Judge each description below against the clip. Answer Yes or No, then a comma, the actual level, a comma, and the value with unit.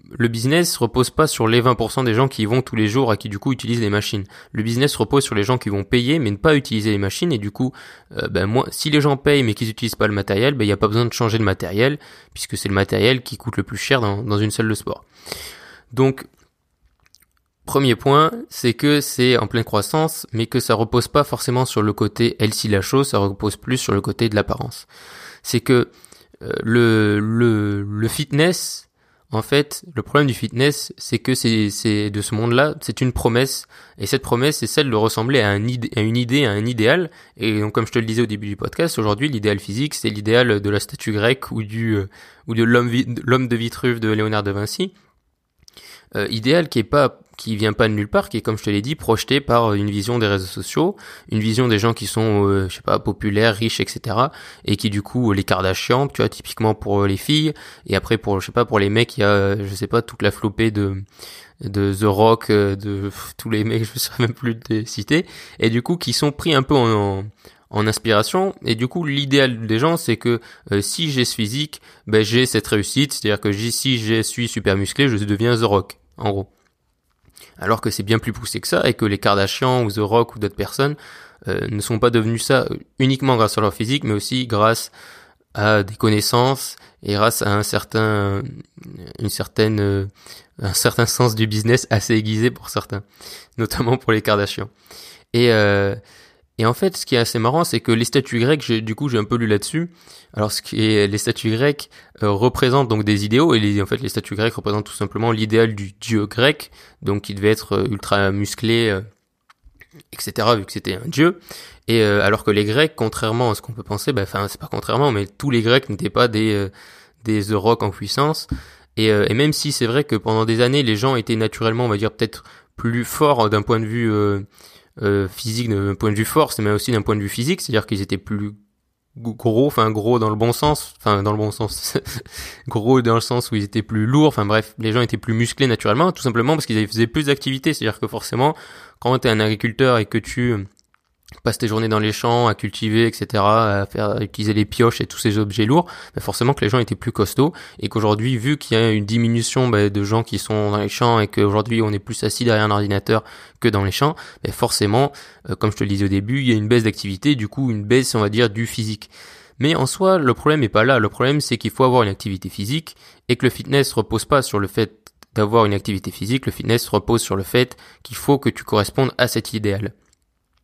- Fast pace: Yes, fast, 235 wpm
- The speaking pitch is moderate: No, low, 115 Hz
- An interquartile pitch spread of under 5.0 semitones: Yes, average, 3.3 semitones